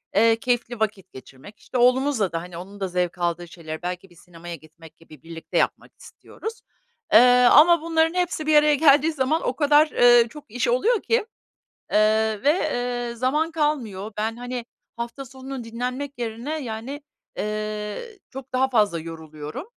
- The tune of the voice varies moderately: No, wide, 6.5 semitones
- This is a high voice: Yes, high, 235 Hz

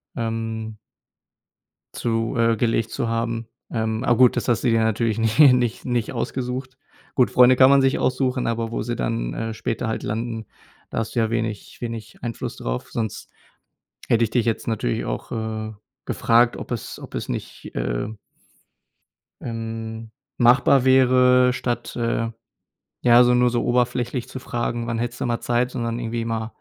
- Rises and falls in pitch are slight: Yes, narrow, 1.6 semitones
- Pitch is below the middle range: Yes, low, 115 Hz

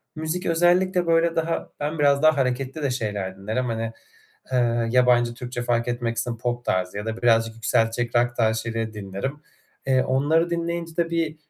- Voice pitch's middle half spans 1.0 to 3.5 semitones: No, wide, 5.5 semitones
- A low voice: Yes, low, 125 Hz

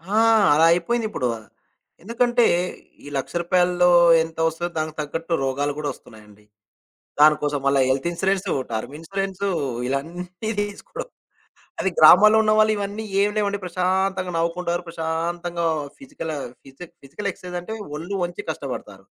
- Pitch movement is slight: No, average, 4.0 semitones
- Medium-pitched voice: Yes, medium, 175 Hz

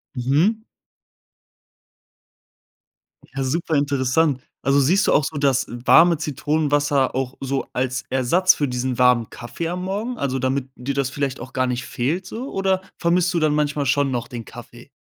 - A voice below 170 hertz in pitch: Yes, medium, 140 Hz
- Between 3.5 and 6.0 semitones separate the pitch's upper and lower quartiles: Yes, average, 4.1 semitones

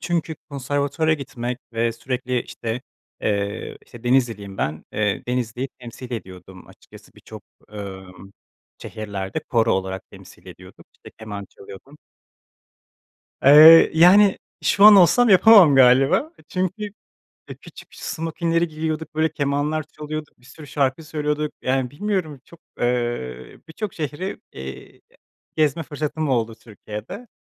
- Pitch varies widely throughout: Yes, wide, 5.8 semitones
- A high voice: No, low, 135 Hz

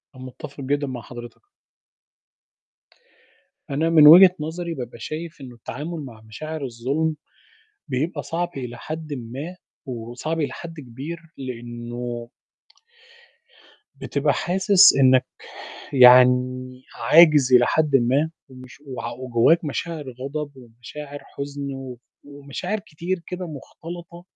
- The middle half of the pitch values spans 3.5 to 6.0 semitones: Yes, average, 4.2 semitones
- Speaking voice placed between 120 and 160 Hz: Yes, medium, 140 Hz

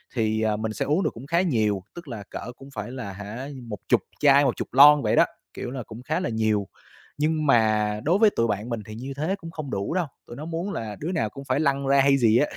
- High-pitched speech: No, low, 130 Hz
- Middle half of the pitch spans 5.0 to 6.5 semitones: Yes, wide, 5.4 semitones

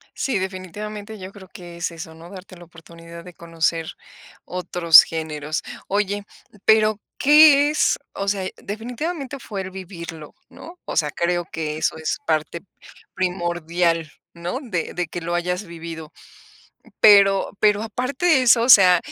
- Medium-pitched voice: Yes, medium, 180 Hz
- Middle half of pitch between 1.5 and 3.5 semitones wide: No, average, 3.9 semitones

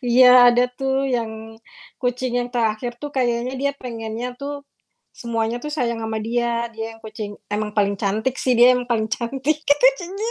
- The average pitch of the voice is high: Yes, high, 240 Hz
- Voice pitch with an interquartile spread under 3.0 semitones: Yes, narrow, 2.4 semitones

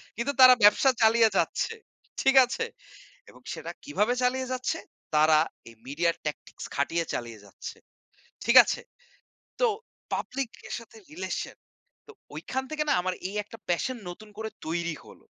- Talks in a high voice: Yes, high, 220 Hz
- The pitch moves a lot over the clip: Yes, wide, 7.3 semitones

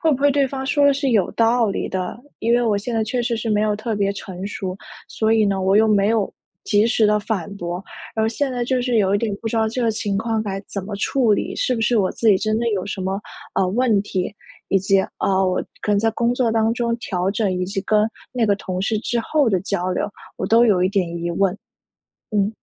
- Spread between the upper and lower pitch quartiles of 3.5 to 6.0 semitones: No, average, 3.1 semitones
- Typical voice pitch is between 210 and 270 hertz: Yes, high, 215 Hz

